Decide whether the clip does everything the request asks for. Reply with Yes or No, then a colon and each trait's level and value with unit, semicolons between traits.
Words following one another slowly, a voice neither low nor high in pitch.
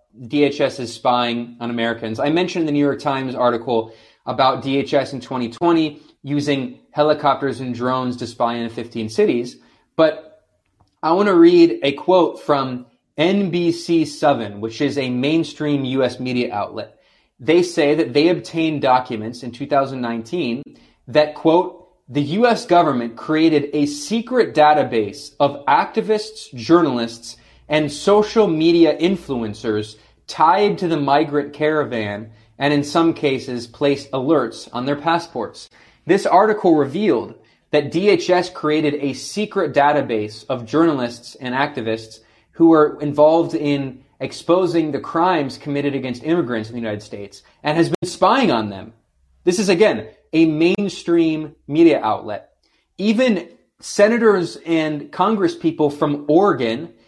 Yes: slow, 130 wpm; medium, 145 Hz